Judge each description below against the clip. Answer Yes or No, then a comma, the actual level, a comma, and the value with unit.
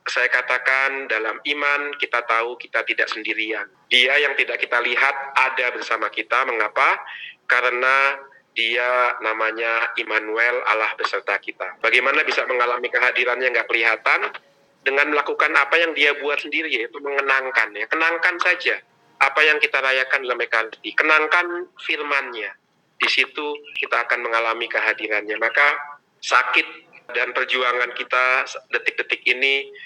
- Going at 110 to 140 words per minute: Yes, average, 130 wpm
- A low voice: Yes, low, 130 Hz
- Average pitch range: Yes, average, 3.0 semitones